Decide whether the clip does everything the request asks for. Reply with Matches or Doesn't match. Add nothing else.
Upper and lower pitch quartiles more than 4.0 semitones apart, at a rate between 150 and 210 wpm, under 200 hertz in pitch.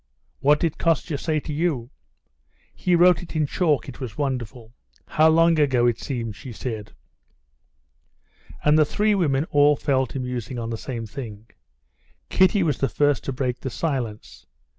Matches